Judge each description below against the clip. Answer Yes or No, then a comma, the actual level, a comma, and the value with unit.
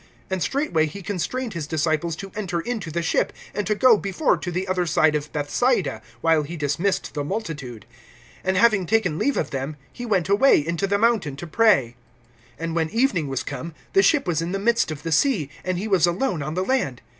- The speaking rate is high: Yes, fast, 215 wpm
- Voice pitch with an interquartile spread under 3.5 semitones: No, average, 5.3 semitones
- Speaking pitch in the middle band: Yes, medium, 175 Hz